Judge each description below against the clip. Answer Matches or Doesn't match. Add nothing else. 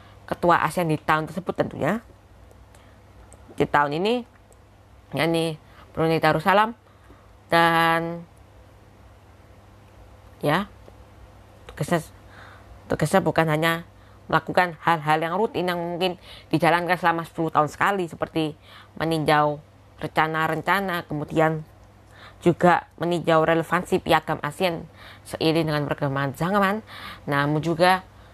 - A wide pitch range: Matches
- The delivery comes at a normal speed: Matches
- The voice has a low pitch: Doesn't match